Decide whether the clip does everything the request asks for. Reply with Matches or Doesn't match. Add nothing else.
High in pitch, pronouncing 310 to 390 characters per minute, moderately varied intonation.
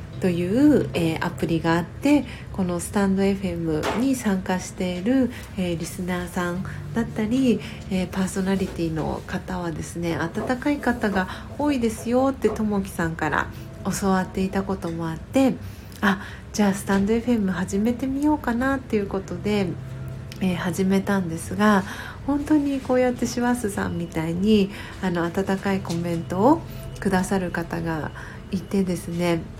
Matches